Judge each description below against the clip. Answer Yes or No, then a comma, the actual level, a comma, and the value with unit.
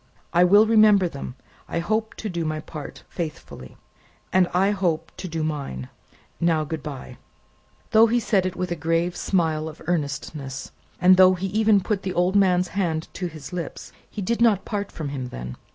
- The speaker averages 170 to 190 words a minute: Yes, average, 185 wpm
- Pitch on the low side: No, medium, 175 Hz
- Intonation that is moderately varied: Yes, average, 3.9 semitones